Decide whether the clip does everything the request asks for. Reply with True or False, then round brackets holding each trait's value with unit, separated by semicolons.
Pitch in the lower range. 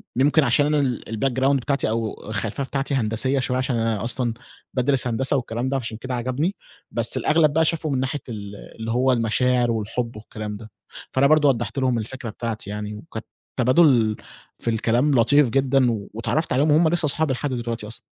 True (125 Hz)